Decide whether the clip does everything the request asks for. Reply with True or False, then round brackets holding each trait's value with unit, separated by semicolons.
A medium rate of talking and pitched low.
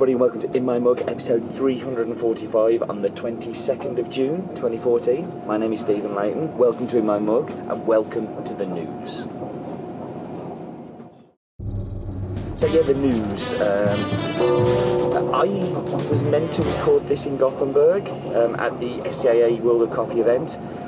True (145 wpm; 115 Hz)